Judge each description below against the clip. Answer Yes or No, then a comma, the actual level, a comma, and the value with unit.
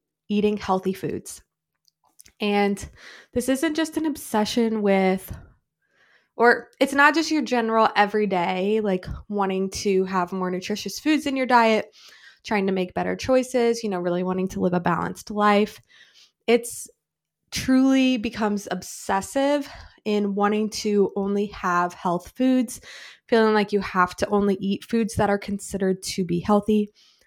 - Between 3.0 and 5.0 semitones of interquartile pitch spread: Yes, average, 3.7 semitones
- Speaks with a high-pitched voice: Yes, high, 210 Hz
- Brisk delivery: No, average, 145 wpm